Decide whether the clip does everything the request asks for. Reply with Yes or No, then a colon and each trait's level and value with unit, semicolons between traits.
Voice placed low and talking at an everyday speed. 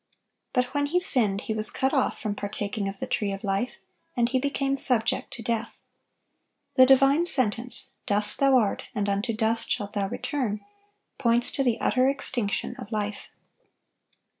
No: high, 235 Hz; average, 165 wpm